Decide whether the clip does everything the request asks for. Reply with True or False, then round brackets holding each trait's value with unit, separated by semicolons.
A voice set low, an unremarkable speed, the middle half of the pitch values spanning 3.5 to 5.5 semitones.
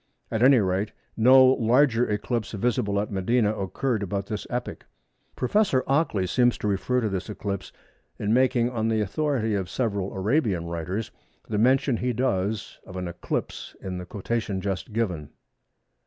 True (110 Hz; 155 wpm; 4.1 semitones)